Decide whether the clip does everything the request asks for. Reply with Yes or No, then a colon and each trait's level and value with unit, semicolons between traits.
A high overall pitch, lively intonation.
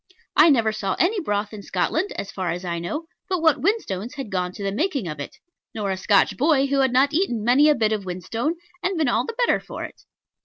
Yes: high, 235 Hz; wide, 8.1 semitones